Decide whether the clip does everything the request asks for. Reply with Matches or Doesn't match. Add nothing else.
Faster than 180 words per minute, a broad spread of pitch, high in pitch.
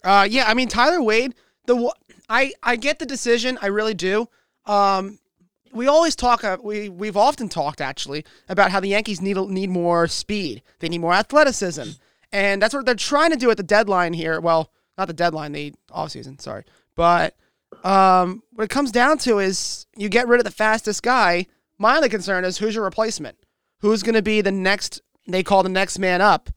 Doesn't match